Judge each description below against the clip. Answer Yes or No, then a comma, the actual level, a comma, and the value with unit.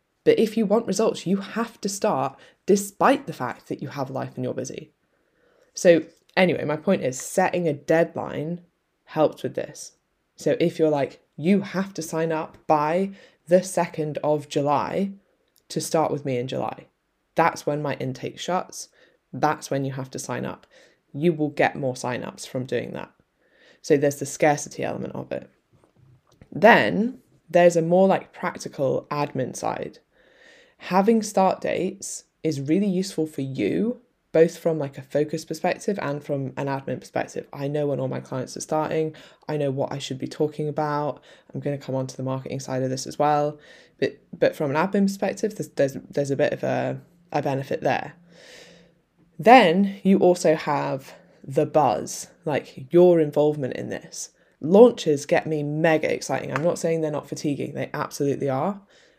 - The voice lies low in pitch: No, medium, 155 Hz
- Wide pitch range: No, average, 4.3 semitones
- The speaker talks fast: No, average, 175 wpm